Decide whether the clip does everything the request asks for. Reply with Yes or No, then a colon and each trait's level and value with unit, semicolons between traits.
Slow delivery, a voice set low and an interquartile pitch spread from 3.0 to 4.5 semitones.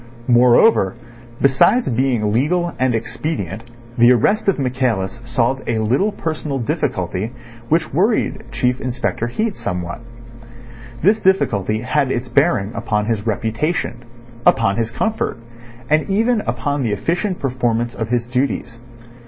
No: slow, 130 wpm; low, 125 Hz; wide, 5.4 semitones